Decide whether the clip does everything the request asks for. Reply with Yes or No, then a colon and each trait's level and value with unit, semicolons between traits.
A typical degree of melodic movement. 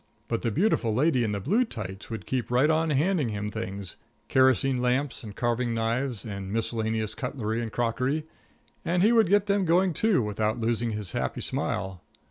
No: wide, 5.7 semitones